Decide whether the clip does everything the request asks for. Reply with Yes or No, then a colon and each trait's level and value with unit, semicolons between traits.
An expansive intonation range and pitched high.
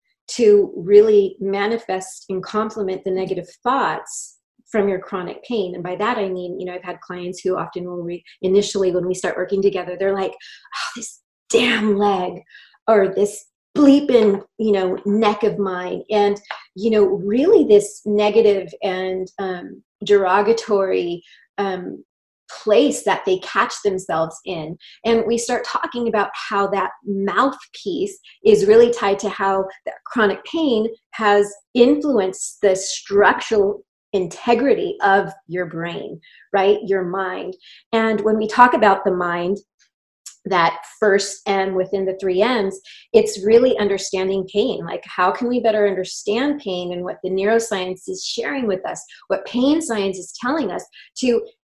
No: average, 3.5 semitones; high, 205 Hz